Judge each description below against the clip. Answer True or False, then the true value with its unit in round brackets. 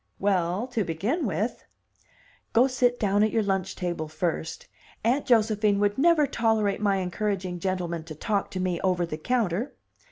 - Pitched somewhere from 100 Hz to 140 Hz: False (200 Hz)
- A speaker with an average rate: True (165 wpm)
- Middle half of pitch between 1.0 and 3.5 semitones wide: False (4.0 semitones)